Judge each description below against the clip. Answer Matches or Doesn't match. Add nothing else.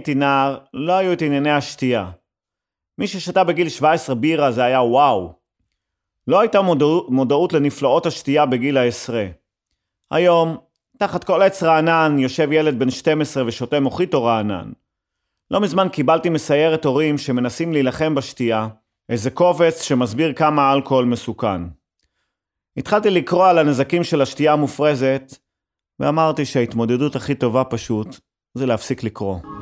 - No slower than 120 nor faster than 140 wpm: Matches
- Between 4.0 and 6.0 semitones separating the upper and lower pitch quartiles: Matches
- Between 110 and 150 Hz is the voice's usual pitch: Matches